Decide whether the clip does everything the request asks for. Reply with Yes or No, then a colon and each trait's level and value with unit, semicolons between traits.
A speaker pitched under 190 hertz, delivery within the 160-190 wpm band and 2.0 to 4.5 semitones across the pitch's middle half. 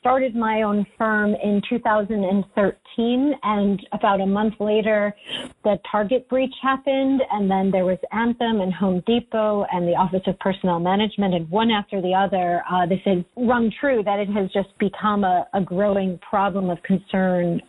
No: high, 205 Hz; average, 170 wpm; average, 2.7 semitones